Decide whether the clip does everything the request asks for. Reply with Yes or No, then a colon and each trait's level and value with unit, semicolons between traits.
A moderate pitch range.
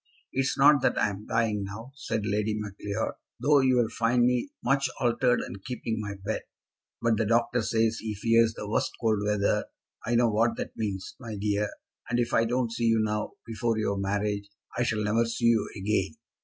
No: narrow, 2.2 semitones